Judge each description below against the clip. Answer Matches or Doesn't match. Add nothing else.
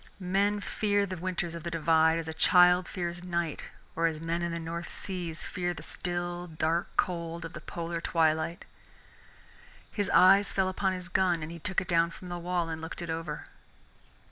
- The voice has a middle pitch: Matches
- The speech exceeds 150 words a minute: Matches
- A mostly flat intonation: Matches